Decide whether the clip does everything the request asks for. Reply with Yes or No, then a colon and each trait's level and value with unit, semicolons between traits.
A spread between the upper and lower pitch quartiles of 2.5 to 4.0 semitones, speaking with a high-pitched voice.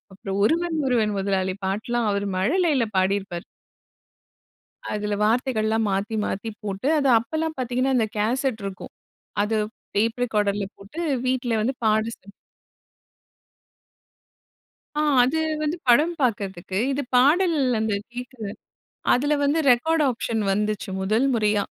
No: average, 4.4 semitones; high, 225 Hz